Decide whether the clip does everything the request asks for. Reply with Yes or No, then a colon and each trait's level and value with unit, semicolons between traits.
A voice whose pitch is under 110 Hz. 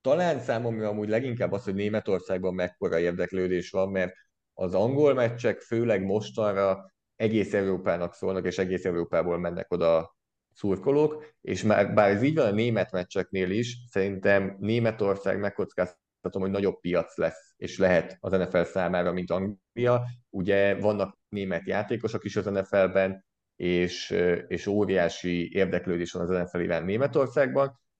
Yes: low, 100 Hz